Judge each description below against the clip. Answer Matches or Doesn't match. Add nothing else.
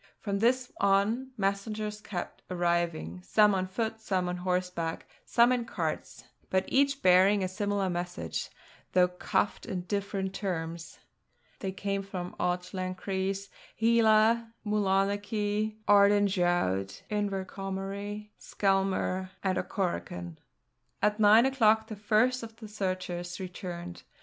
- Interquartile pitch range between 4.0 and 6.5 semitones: Doesn't match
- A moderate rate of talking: Doesn't match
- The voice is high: Matches